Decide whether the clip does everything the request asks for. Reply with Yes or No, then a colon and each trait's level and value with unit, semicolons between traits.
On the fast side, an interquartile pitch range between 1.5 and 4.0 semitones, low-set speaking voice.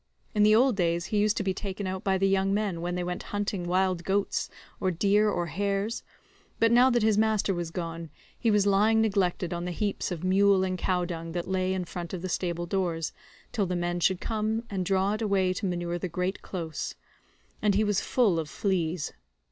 No: fast, 220 wpm; average, 2.8 semitones; high, 190 Hz